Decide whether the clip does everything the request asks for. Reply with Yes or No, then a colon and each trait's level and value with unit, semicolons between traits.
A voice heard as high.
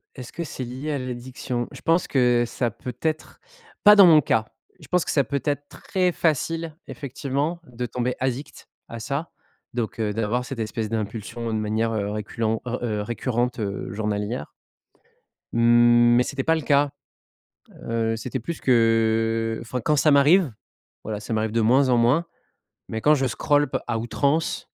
No: low, 120 Hz